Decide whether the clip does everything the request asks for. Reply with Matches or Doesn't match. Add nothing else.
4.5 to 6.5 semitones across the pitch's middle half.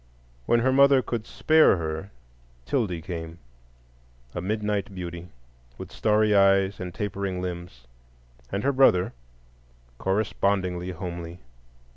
Doesn't match